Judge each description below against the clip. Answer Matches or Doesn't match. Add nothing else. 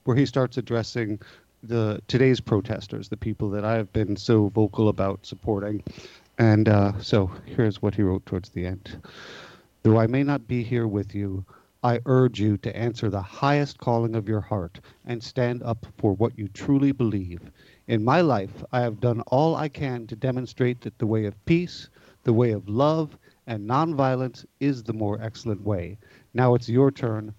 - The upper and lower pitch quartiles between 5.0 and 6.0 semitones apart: Doesn't match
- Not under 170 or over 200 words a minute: Matches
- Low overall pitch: Matches